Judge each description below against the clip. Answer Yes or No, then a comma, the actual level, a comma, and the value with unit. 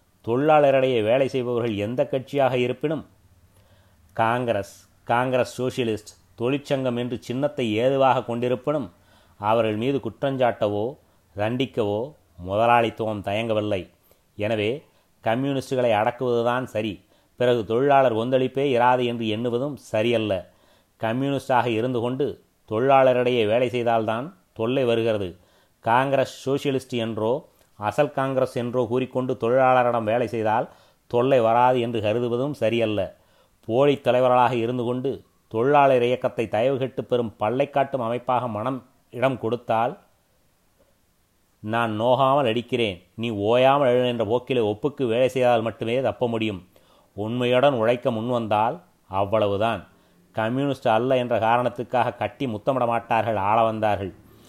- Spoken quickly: No, average, 100 wpm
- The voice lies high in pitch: No, low, 120 Hz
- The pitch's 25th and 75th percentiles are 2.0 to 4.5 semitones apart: Yes, average, 2.9 semitones